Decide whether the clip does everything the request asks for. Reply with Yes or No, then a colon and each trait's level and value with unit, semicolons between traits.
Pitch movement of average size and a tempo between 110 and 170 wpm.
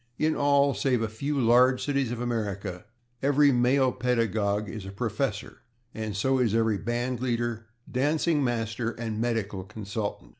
Yes: average, 3.2 semitones; average, 150 wpm